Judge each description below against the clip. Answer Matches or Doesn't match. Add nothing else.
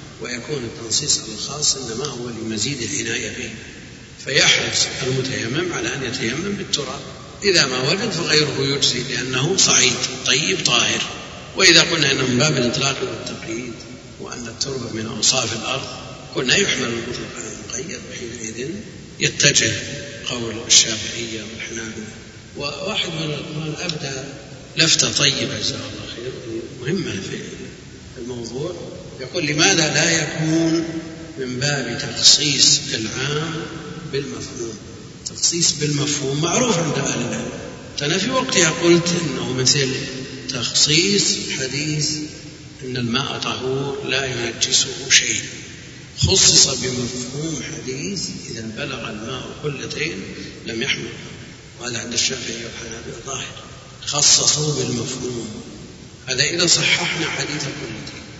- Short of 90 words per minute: Doesn't match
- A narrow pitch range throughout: Doesn't match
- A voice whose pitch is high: Doesn't match